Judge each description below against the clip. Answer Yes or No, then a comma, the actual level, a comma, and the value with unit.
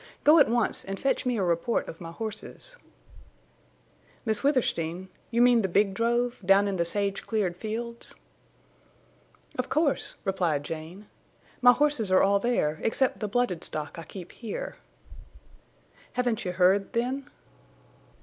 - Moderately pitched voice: No, high, 210 Hz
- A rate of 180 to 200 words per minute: No, average, 140 wpm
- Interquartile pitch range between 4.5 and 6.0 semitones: Yes, average, 5.0 semitones